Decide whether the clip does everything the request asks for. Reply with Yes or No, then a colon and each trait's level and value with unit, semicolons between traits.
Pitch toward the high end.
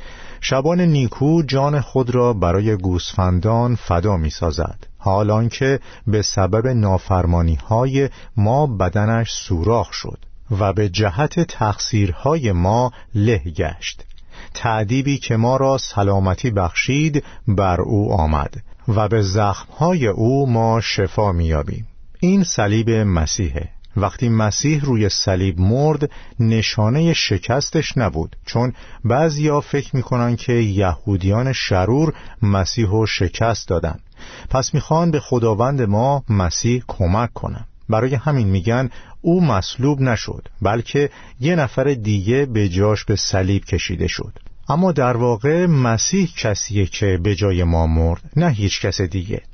No: low, 110 Hz